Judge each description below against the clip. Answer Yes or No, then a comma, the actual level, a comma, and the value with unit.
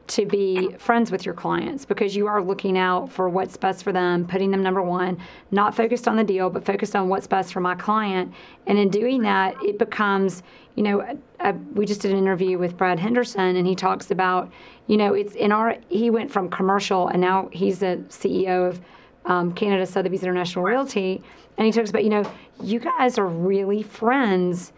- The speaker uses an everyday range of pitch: No, narrow, 2.3 semitones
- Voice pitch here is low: No, high, 195 Hz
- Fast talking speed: Yes, fast, 210 wpm